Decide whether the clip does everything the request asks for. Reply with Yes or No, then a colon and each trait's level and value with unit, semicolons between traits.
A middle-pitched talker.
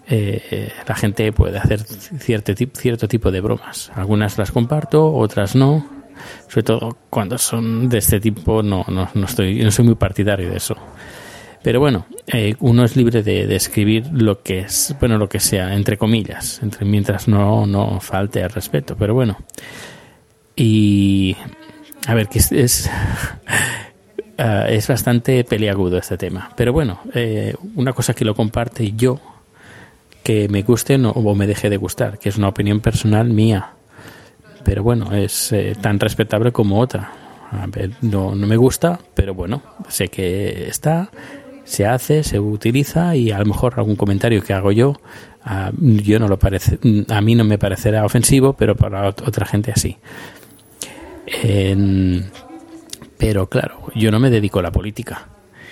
No: low, 110 Hz